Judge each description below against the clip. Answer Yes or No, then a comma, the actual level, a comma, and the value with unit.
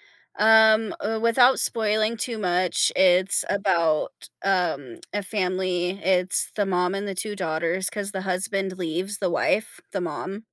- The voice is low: No, high, 190 Hz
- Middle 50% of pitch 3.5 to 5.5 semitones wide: No, average, 2.7 semitones